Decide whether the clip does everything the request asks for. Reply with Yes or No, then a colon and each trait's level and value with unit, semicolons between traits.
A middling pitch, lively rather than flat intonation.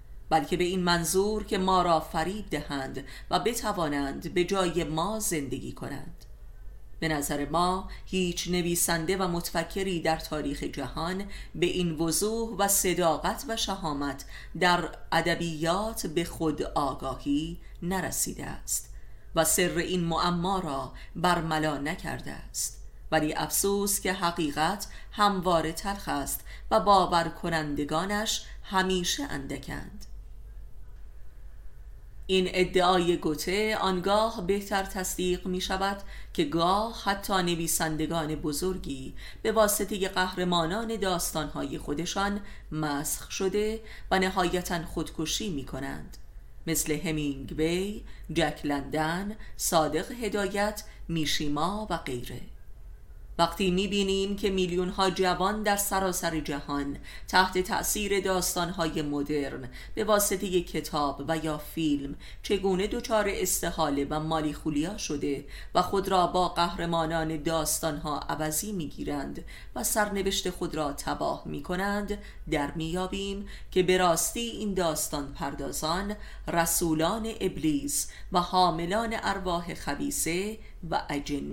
No: medium, 175 Hz; average, 3.7 semitones